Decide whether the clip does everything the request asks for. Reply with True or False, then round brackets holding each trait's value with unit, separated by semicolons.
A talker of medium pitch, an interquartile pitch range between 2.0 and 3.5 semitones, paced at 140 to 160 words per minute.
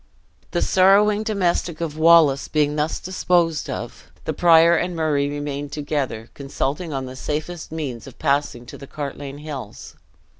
True (150 Hz; 3.2 semitones; 150 wpm)